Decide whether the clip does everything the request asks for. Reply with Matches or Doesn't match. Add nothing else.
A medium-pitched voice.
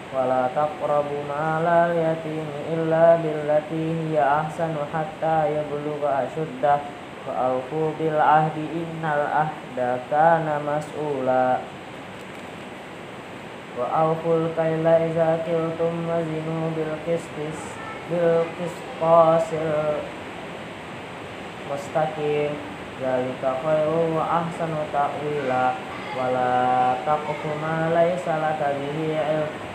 Matches